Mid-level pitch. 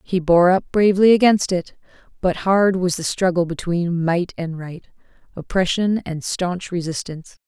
Yes: medium, 180 Hz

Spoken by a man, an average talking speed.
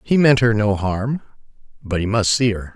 Yes: male; average, 195 wpm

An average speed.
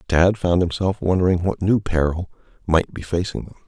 Yes: average, 180 wpm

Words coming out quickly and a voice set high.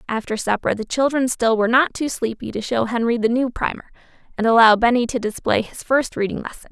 Yes: fast, 215 wpm; high, 235 Hz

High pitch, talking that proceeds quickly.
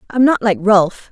Yes: high, 220 Hz; fast, 215 wpm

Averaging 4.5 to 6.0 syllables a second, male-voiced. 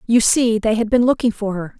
No: 5.5 syllables/s; female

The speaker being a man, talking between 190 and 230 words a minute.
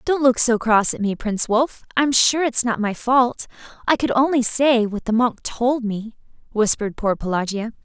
No: female; average, 200 wpm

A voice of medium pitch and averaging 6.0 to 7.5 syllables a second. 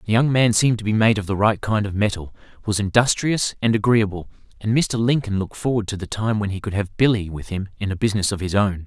No: low, 105 Hz; 6.3 syllables/s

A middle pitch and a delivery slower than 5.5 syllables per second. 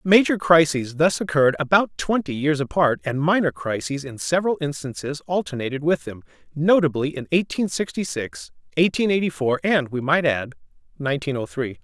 Yes: medium, 150 Hz; 5.3 syllables/s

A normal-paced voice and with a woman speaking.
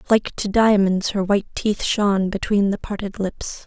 Yes: average, 180 wpm; female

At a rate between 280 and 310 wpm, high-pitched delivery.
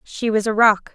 No: fast, 255 wpm; high, 215 Hz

